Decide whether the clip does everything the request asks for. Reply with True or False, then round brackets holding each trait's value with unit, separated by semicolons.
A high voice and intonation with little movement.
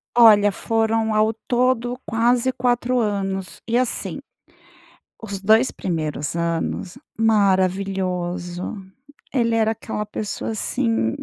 False (215 Hz; 3.5 semitones)